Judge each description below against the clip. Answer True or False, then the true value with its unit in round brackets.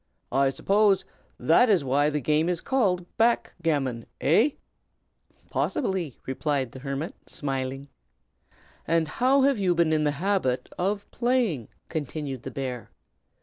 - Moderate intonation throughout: False (6.6 semitones)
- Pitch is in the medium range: True (155 Hz)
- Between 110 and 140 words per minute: True (135 wpm)